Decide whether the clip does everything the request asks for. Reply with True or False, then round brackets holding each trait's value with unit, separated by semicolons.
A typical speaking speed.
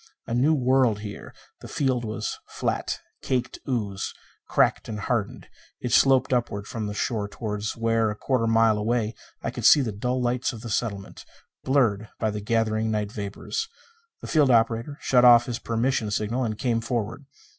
True (180 wpm)